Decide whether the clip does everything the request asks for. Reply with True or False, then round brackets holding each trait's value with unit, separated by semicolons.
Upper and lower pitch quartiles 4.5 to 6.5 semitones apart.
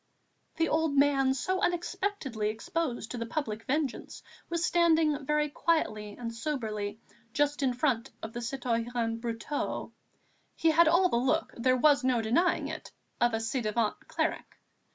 True (5.3 semitones)